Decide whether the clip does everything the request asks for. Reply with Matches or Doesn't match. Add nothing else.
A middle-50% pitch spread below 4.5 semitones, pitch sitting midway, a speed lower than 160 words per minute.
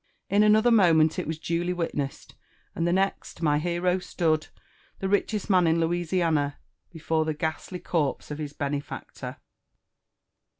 Matches